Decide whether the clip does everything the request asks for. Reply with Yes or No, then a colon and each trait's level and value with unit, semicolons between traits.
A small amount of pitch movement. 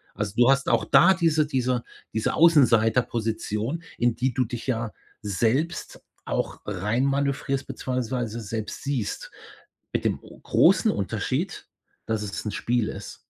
No: average, 3.8 semitones